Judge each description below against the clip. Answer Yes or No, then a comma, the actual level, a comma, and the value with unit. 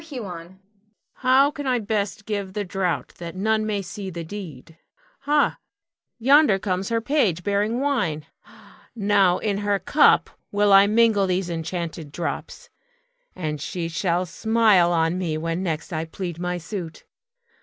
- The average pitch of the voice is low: No, high, 195 Hz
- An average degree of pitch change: Yes, average, 4.1 semitones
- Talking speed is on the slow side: No, average, 150 wpm